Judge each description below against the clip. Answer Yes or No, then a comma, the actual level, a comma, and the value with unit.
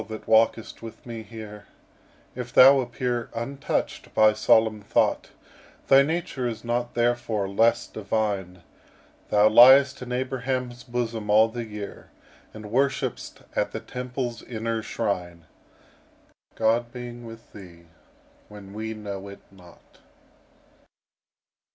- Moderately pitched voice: No, low, 115 Hz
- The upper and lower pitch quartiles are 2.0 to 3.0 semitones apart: Yes, narrow, 2.6 semitones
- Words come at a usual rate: No, slow, 120 wpm